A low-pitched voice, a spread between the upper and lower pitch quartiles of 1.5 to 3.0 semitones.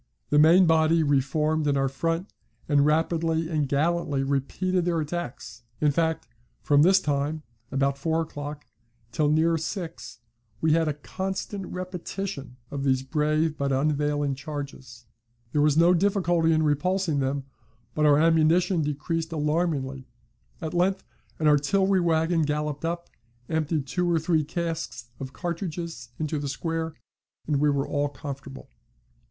No: medium, 155 Hz; narrow, 2.6 semitones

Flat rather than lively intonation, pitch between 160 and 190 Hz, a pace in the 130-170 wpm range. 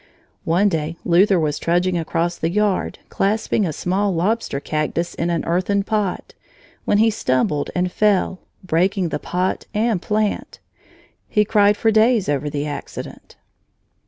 No: average, 3.9 semitones; medium, 185 Hz; average, 145 wpm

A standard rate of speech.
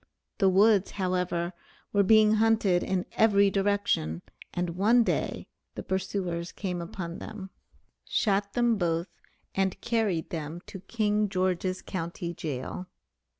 No: slow, 125 wpm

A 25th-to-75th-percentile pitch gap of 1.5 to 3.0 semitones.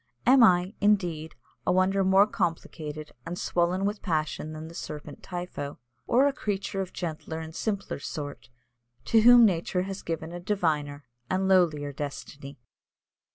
No: average, 3.9 semitones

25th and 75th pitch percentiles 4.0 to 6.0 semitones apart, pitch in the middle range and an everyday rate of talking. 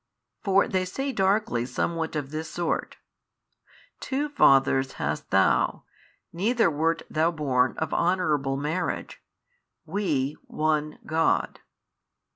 No: average, 4.3 semitones; medium, 160 Hz; slow, 105 wpm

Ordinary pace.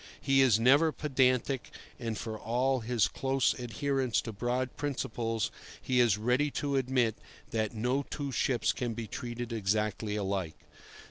Yes: average, 145 wpm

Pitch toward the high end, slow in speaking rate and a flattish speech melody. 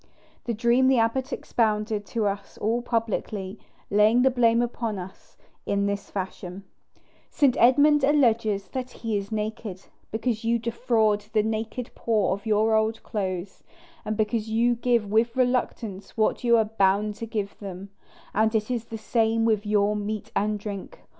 No: high, 220 Hz; average, 160 wpm; narrow, 2.2 semitones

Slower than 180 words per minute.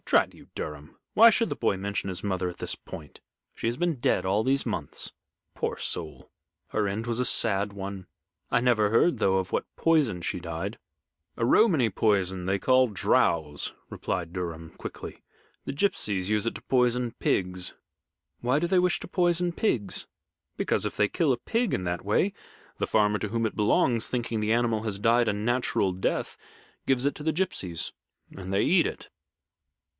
No: average, 185 wpm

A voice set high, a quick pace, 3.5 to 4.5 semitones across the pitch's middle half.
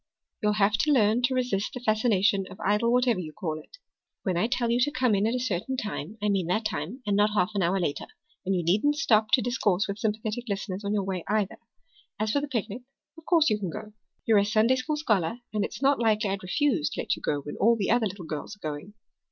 Yes: high, 210 Hz; fast, 250 wpm; average, 3.9 semitones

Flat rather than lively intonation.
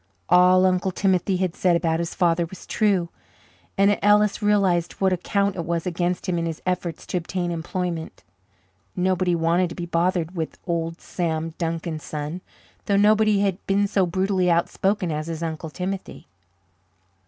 Yes: narrow, 2.2 semitones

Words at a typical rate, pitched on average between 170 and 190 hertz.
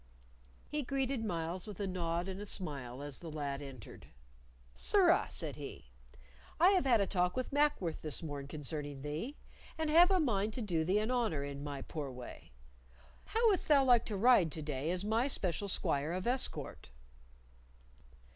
Yes: average, 175 wpm; medium, 185 Hz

